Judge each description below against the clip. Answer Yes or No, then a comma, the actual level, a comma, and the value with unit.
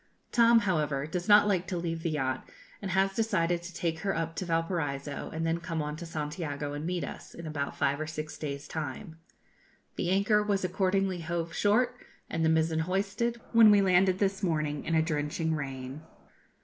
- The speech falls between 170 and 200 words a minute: Yes, average, 190 wpm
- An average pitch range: Yes, average, 3.9 semitones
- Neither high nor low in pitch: Yes, medium, 165 Hz